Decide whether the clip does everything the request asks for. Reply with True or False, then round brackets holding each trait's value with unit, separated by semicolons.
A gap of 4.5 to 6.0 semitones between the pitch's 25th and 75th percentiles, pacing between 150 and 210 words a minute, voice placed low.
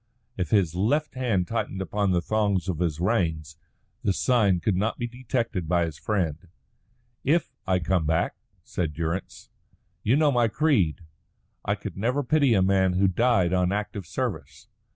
True (4.9 semitones; 165 wpm; 95 Hz)